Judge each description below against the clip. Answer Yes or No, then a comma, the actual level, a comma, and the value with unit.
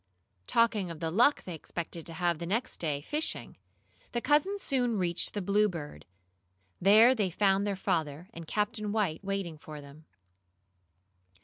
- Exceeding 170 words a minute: No, average, 150 wpm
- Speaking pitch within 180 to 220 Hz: Yes, high, 190 Hz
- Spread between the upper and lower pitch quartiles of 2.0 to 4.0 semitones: No, average, 4.6 semitones